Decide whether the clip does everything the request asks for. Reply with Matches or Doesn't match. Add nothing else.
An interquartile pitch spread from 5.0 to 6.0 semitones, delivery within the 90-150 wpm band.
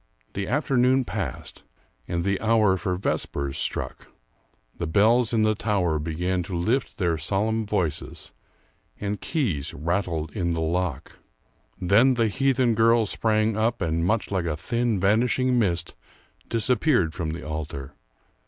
Matches